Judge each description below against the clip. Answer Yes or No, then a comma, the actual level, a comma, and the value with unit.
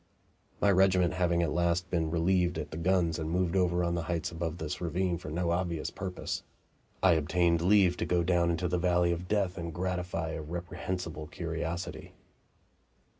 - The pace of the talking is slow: No, average, 175 wpm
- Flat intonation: Yes, narrow, 1.4 semitones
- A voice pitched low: Yes, very low, 85 Hz